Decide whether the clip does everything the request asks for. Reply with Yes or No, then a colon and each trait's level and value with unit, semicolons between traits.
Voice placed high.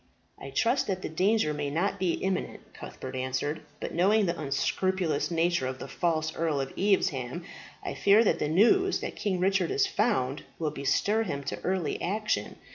No: medium, 175 Hz